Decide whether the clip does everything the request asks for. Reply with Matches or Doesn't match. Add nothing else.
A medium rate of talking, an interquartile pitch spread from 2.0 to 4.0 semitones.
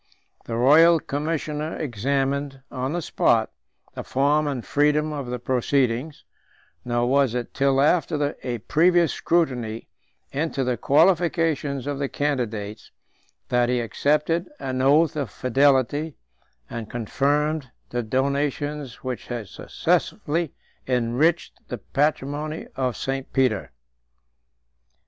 Doesn't match